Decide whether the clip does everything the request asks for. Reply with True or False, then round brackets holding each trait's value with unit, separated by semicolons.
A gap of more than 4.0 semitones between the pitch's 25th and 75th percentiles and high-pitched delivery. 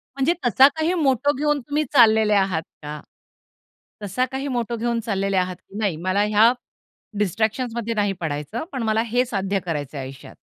True (4.6 semitones; 220 Hz)